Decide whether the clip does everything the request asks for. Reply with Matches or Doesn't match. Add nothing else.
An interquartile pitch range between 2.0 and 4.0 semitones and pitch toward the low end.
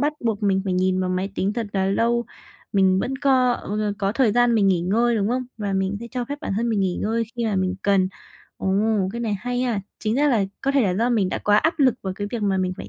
Doesn't match